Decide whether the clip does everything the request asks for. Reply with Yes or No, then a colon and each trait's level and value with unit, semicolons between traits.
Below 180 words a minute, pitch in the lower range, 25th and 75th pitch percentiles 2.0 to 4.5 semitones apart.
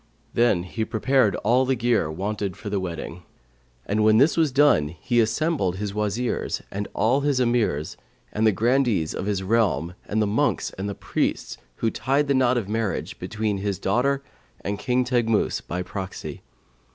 Yes: average, 170 wpm; low, 110 Hz; average, 4.2 semitones